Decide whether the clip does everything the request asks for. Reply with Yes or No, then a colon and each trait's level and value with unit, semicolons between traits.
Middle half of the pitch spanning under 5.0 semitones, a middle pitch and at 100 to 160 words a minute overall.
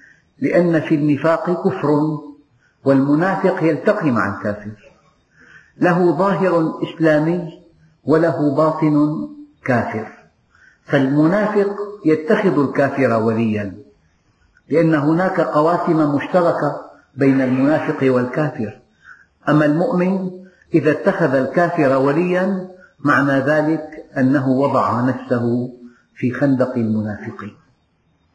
No: average, 4.5 semitones; medium, 150 Hz; average, 85 wpm